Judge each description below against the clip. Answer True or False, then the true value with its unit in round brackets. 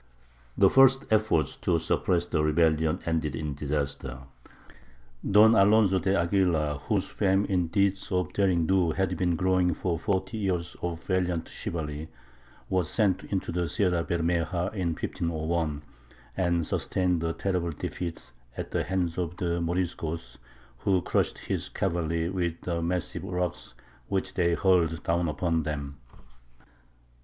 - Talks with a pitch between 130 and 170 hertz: False (85 Hz)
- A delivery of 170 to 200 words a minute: False (140 wpm)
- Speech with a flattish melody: True (2.3 semitones)